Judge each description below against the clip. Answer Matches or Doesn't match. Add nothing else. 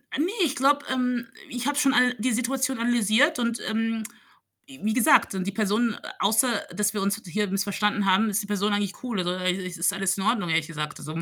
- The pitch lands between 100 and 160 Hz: Doesn't match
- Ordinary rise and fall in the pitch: Matches